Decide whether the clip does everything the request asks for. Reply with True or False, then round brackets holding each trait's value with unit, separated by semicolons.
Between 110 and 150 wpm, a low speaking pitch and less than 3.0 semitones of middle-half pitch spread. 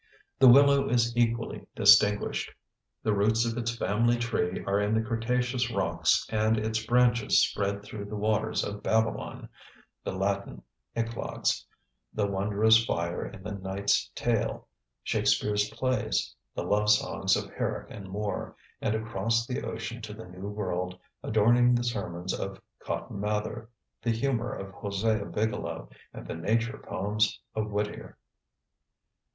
True (140 wpm; 110 Hz; 2.4 semitones)